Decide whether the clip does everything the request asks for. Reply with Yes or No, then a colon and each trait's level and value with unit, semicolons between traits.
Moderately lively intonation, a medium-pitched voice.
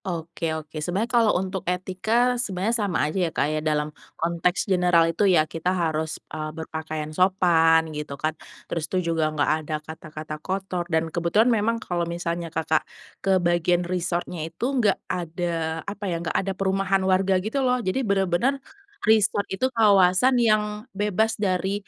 Yes: average, 3.6 semitones; medium, 180 Hz